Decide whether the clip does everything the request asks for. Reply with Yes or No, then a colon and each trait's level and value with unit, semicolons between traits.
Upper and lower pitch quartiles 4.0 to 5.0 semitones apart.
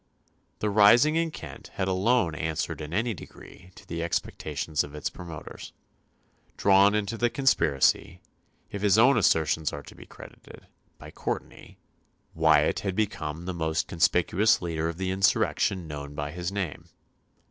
Yes: average, 4.5 semitones